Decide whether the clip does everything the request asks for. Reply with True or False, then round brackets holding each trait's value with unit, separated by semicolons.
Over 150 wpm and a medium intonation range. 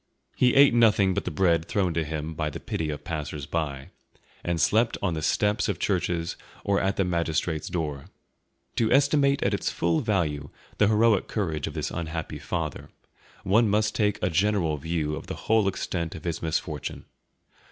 True (180 wpm; 4.9 semitones)